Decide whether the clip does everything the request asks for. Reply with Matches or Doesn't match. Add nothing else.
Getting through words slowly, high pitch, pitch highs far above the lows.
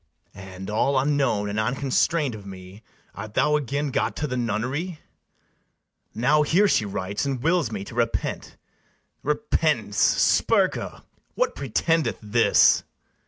Doesn't match